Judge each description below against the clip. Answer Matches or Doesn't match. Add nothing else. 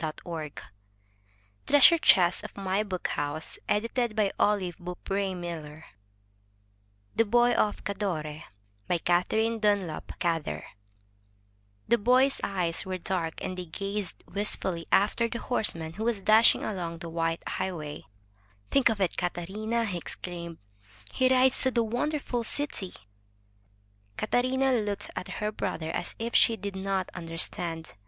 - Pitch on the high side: Matches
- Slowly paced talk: Matches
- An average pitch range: Matches